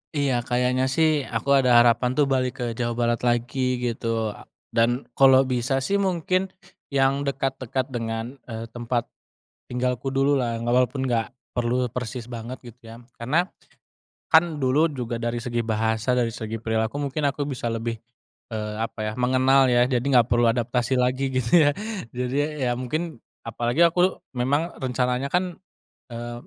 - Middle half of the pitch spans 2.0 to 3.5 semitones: Yes, narrow, 2.4 semitones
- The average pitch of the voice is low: Yes, low, 125 Hz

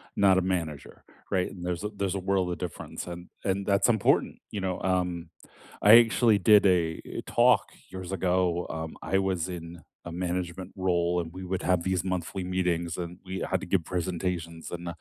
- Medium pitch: No, very low, 90 Hz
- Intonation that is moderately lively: No, narrow, 1.6 semitones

